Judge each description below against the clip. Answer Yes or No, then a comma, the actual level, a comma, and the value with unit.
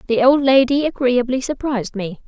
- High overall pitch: Yes, very high, 255 Hz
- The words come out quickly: No, average, 160 wpm